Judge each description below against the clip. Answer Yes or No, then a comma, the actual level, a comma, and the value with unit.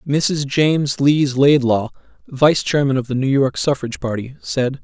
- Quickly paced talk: No, average, 160 wpm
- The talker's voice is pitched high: No, low, 135 Hz